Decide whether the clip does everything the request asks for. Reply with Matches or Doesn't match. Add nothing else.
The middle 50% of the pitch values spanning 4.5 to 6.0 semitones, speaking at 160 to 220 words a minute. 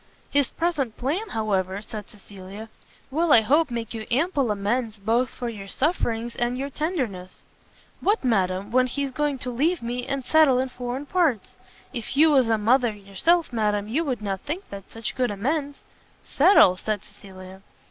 Matches